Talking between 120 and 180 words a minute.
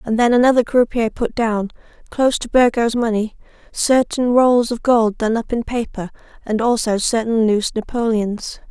Yes: average, 160 wpm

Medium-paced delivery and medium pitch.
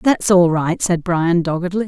Yes: average, 195 wpm; medium, 175 Hz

